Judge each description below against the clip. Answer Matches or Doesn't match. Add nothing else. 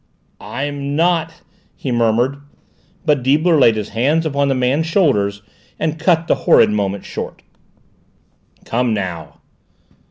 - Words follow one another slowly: Matches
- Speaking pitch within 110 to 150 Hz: Matches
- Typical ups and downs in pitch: Doesn't match